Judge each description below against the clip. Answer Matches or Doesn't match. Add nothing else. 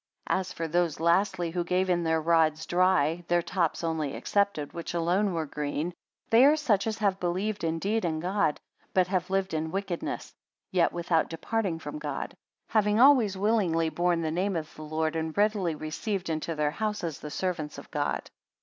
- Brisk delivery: Doesn't match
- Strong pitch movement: Doesn't match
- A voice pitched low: Doesn't match